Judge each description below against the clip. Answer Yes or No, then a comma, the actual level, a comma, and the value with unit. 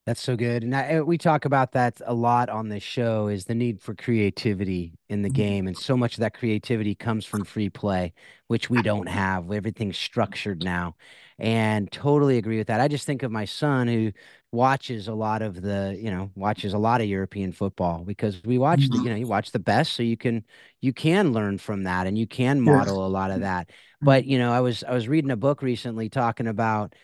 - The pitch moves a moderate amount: Yes, average, 3.6 semitones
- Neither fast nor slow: No, fast, 230 wpm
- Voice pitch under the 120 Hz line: Yes, low, 110 Hz